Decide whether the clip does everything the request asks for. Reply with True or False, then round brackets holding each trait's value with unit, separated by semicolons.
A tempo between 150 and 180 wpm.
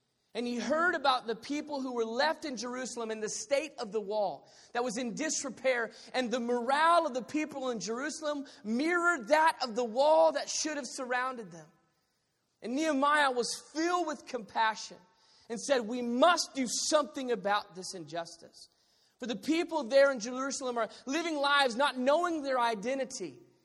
True (170 wpm)